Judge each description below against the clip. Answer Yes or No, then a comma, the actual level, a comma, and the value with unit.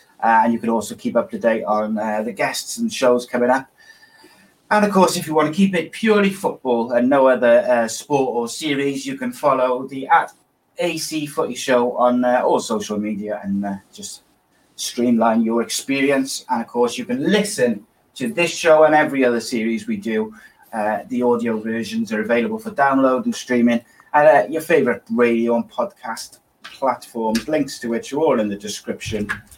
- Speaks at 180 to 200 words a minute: Yes, average, 195 wpm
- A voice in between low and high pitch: No, low, 125 Hz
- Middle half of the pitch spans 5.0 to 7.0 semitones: Yes, average, 5.3 semitones